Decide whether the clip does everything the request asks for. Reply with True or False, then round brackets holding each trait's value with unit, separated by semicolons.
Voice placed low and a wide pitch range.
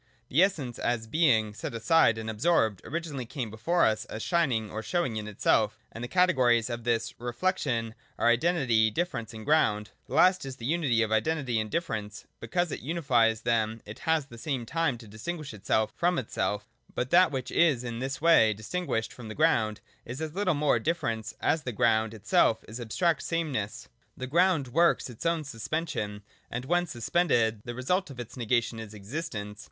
True (120 Hz; 6.4 semitones)